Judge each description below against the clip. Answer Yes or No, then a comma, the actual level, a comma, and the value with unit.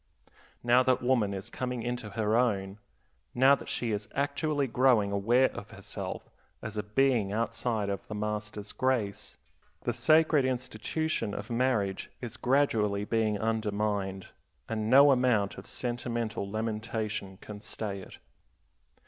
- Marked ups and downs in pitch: No, average, 3.4 semitones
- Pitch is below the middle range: Yes, low, 110 Hz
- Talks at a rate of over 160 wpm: No, slow, 135 wpm